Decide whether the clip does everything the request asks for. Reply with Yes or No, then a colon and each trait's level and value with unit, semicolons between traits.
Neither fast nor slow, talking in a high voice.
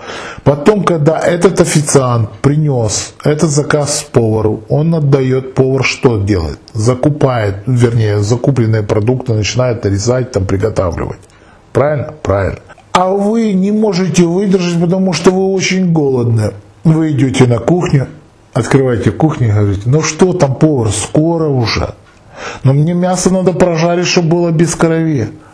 No: average, 130 wpm; medium, 140 Hz